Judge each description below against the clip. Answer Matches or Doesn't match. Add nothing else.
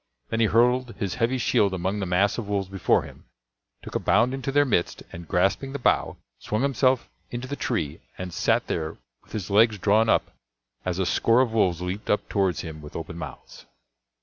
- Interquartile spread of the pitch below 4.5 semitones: Doesn't match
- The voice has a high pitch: Doesn't match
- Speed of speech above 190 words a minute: Matches